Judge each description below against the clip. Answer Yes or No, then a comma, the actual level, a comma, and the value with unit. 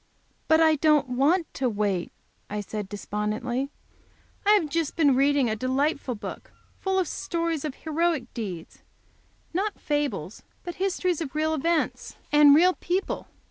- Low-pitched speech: No, very high, 295 Hz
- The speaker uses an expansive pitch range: No, average, 5.0 semitones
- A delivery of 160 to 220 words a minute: No, average, 145 wpm